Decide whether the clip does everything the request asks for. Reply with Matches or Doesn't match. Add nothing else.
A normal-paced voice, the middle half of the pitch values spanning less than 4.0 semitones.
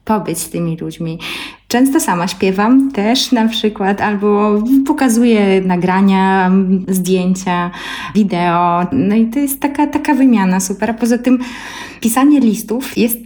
Doesn't match